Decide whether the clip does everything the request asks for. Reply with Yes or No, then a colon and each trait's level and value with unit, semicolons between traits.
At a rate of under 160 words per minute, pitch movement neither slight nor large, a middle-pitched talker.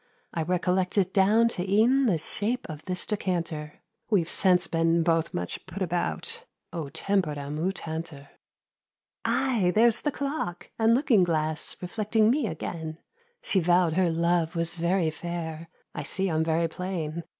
Yes: average, 150 wpm; average, 3.7 semitones; medium, 175 Hz